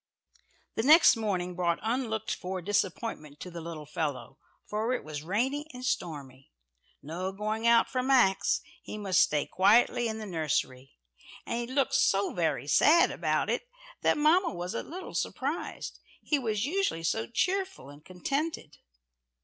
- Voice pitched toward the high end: Yes, high, 200 Hz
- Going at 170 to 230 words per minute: No, average, 155 wpm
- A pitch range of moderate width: No, wide, 7.5 semitones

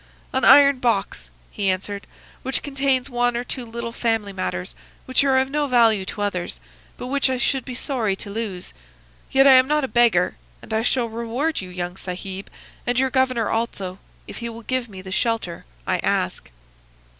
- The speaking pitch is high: Yes, high, 235 Hz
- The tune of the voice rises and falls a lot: No, average, 4.8 semitones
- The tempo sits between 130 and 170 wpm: No, average, 190 wpm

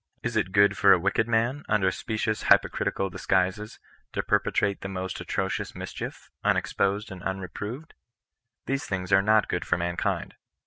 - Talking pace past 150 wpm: Yes, average, 160 wpm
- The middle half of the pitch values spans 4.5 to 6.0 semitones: No, narrow, 2.5 semitones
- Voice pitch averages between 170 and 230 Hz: No, low, 100 Hz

